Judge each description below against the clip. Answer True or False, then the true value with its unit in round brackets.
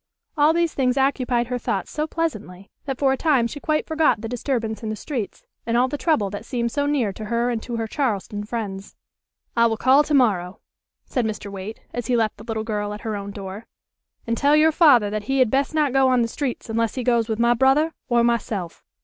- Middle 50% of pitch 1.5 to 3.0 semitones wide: False (3.9 semitones)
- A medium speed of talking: False (235 wpm)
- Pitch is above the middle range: True (235 Hz)